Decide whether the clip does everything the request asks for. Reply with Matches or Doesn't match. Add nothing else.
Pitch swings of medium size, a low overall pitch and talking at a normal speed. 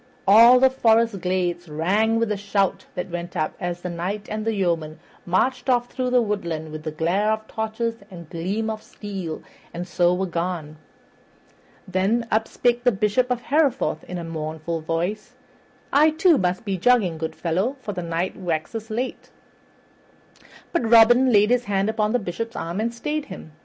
Doesn't match